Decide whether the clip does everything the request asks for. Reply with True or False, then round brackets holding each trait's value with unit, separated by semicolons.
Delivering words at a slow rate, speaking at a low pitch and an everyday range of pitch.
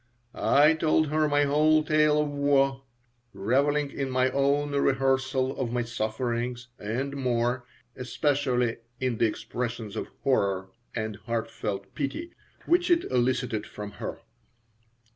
True (125 wpm; 130 Hz; 3.4 semitones)